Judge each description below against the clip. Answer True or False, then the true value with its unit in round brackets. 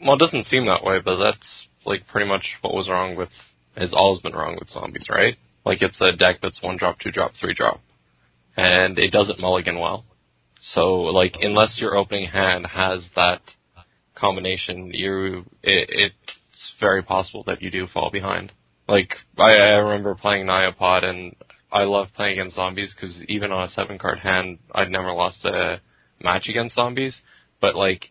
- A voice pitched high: False (95 Hz)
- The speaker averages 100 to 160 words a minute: False (180 wpm)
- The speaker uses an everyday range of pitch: False (1.9 semitones)